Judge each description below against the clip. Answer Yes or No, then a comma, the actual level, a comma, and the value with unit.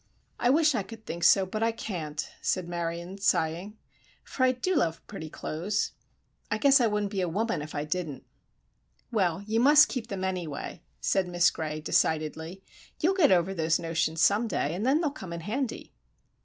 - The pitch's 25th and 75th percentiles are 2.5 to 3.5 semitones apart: No, wide, 5.5 semitones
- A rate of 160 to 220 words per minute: Yes, average, 185 wpm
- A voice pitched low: No, high, 190 Hz